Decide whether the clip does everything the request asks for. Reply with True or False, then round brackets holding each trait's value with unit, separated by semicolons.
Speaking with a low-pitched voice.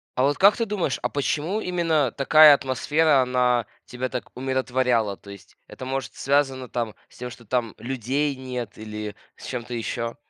True (130 Hz)